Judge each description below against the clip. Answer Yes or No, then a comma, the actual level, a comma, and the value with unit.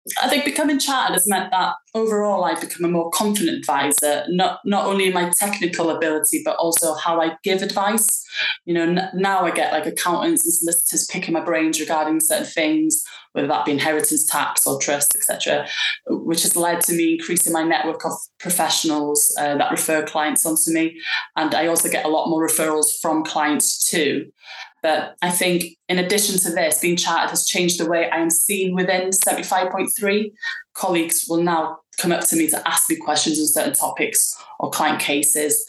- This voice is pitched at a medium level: Yes, medium, 170 Hz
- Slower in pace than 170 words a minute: No, average, 190 wpm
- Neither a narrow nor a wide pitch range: Yes, average, 3.2 semitones